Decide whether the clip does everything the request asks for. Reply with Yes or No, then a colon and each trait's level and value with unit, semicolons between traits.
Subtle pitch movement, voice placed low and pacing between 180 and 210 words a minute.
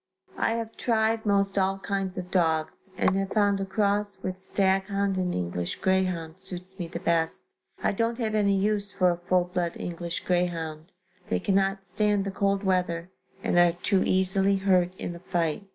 No: narrow, 2.2 semitones; high, 190 Hz; average, 185 wpm